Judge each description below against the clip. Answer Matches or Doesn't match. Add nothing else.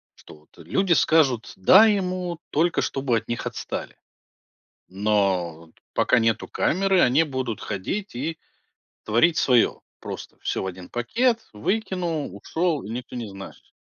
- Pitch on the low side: Matches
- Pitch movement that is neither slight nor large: Doesn't match